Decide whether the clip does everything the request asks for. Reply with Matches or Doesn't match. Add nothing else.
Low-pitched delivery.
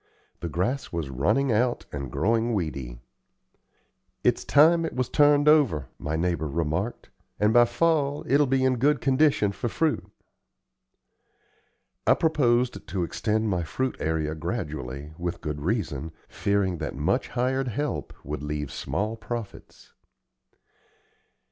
Matches